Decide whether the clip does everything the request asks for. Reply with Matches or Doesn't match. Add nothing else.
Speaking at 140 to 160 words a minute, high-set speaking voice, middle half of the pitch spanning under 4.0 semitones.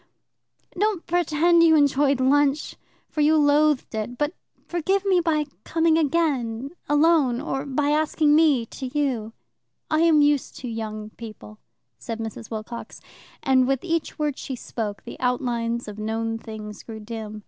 Doesn't match